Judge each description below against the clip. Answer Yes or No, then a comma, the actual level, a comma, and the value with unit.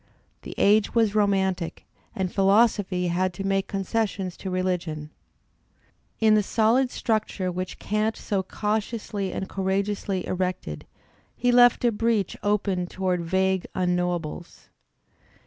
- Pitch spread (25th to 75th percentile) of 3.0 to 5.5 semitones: No, narrow, 2.6 semitones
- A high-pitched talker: Yes, high, 195 Hz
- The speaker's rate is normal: No, slow, 120 wpm